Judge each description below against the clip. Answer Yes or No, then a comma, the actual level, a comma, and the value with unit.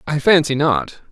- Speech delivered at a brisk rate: No, average, 160 wpm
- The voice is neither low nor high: Yes, medium, 145 Hz